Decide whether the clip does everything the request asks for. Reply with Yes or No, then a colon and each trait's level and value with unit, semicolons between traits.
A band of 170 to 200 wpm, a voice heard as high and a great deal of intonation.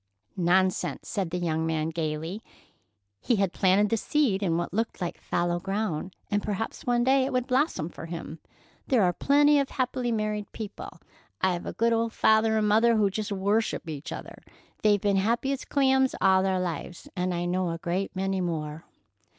No: average, 185 wpm; high, 195 Hz; average, 4.6 semitones